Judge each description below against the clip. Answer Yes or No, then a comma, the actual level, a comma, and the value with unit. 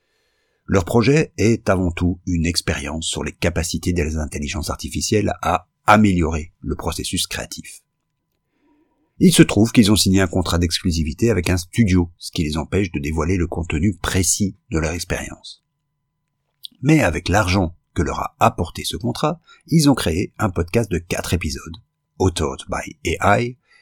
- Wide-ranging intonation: Yes, wide, 5.8 semitones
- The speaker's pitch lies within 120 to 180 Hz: No, very low, 95 Hz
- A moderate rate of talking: Yes, average, 155 wpm